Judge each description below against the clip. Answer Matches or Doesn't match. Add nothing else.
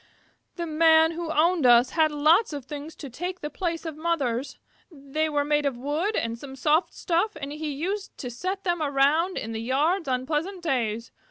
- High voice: Matches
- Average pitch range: Matches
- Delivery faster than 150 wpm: Matches